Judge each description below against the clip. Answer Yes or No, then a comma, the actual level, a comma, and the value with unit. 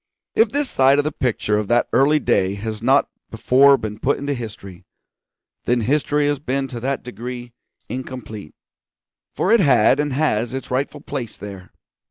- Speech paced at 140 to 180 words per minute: Yes, average, 170 wpm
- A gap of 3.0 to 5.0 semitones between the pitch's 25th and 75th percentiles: Yes, average, 4.2 semitones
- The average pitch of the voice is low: Yes, low, 125 Hz